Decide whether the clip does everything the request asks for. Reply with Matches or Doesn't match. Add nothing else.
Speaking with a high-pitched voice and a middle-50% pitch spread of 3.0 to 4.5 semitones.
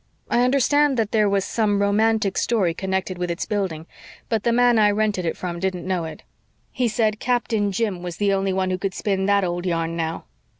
Matches